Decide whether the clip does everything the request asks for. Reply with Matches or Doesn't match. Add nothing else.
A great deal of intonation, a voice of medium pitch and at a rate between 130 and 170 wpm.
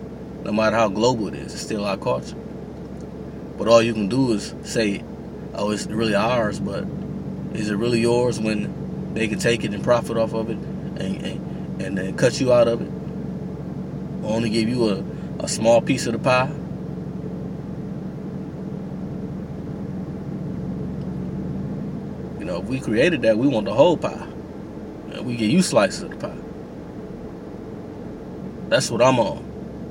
Matches